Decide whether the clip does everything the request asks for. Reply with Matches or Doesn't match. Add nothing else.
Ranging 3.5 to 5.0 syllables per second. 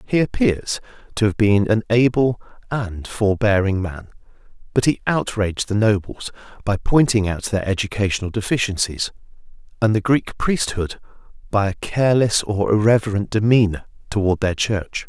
Matches